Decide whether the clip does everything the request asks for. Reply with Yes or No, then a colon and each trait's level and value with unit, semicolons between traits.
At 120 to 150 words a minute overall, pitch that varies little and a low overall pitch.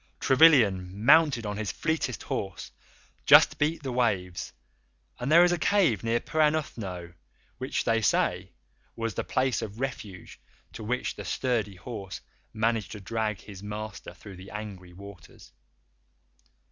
No: average, 140 wpm; average, 4.9 semitones; low, 110 Hz